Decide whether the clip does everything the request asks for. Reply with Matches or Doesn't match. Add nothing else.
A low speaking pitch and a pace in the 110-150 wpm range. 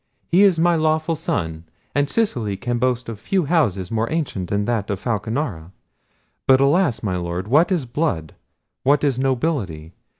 Doesn't match